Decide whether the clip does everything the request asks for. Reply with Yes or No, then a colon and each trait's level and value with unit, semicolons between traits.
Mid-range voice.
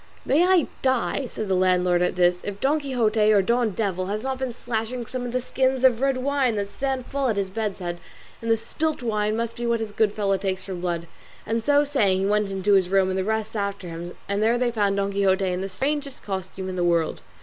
No: high, 215 Hz